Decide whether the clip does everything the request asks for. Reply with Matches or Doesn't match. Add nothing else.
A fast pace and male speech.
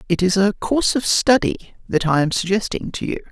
Matches